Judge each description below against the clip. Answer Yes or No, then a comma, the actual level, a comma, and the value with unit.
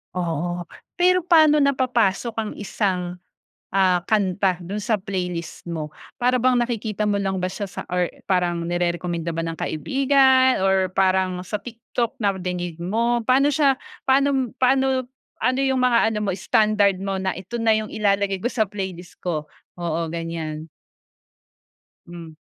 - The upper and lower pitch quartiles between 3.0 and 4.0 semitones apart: No, wide, 5.4 semitones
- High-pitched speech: Yes, high, 195 Hz